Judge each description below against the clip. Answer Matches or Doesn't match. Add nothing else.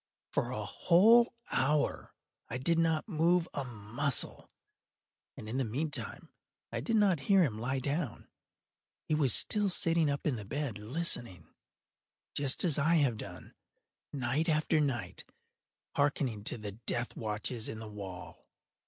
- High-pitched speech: Doesn't match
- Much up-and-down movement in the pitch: Matches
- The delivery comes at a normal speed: Matches